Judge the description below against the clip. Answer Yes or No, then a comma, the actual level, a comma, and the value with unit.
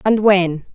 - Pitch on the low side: No, high, 190 Hz